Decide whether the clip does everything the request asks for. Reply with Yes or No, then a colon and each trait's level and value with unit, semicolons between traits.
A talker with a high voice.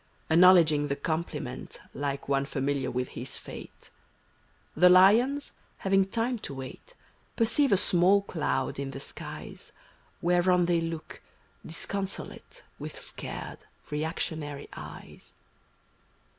No: medium, 170 Hz